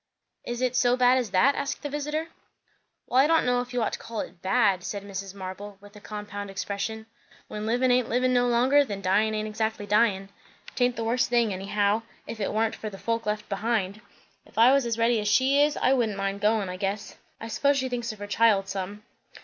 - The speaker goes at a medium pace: No, fast, 225 wpm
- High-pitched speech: Yes, high, 220 Hz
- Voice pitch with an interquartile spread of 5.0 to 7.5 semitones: No, average, 3.5 semitones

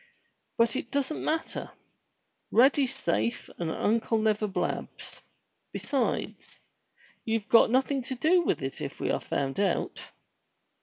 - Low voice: No, high, 230 Hz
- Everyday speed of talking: No, slow, 130 wpm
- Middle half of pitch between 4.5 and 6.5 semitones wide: Yes, average, 4.8 semitones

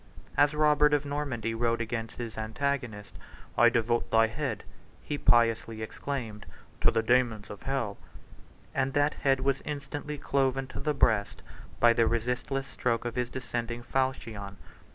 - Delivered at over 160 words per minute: No, average, 150 wpm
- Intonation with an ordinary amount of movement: Yes, average, 3.3 semitones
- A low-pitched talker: Yes, low, 120 Hz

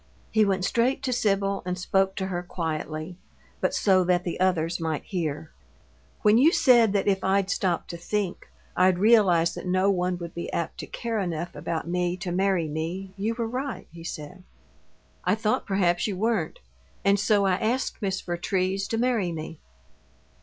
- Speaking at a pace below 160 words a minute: No, average, 180 wpm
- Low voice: No, medium, 185 Hz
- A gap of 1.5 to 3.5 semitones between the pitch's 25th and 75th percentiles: Yes, average, 2.9 semitones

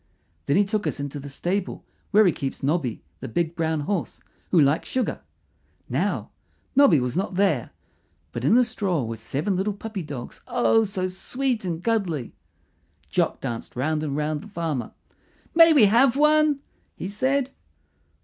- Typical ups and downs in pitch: No, wide, 6.9 semitones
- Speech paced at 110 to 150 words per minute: No, average, 165 wpm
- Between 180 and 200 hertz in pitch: Yes, medium, 185 Hz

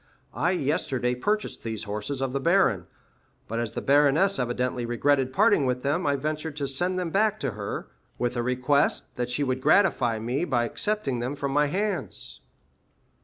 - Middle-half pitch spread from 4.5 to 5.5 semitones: No, average, 4.1 semitones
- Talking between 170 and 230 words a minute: Yes, average, 175 wpm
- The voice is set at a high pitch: No, low, 135 Hz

